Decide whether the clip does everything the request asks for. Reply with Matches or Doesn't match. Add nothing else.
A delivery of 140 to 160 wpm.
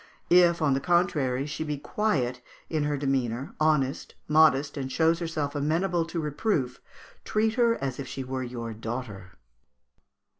Matches